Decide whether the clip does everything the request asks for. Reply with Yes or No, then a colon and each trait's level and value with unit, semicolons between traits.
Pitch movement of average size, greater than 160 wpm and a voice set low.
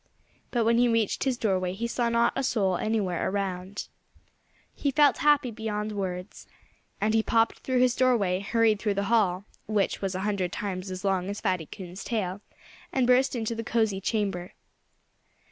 No: average, 3.6 semitones; average, 175 wpm; high, 210 Hz